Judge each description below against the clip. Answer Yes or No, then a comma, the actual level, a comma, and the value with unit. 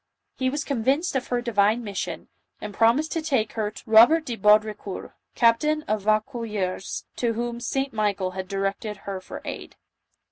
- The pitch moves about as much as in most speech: Yes, average, 3.7 semitones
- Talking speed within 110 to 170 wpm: Yes, average, 165 wpm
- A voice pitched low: No, high, 225 Hz